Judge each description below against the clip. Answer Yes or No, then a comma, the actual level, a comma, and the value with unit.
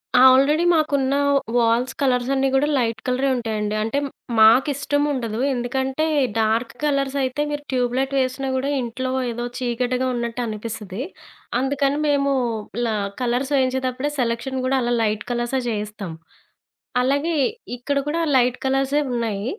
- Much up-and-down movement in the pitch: No, average, 2.7 semitones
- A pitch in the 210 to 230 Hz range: No, very high, 255 Hz